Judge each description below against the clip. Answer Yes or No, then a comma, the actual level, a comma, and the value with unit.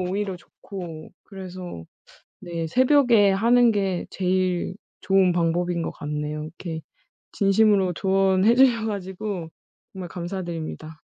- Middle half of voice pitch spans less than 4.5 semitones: Yes, average, 2.8 semitones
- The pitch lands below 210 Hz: Yes, medium, 185 Hz